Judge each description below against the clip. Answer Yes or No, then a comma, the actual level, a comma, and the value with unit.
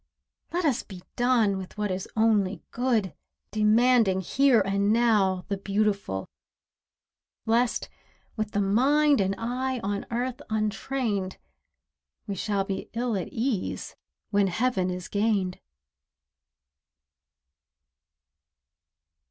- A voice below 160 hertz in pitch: No, high, 210 Hz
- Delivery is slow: Yes, slow, 105 wpm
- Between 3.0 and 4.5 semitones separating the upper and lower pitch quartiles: Yes, average, 3.7 semitones